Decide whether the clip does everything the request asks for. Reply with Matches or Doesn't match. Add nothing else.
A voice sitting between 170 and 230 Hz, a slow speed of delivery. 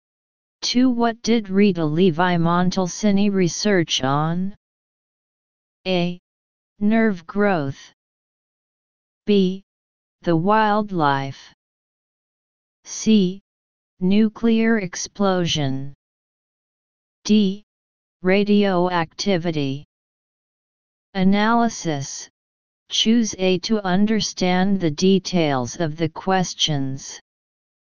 Matches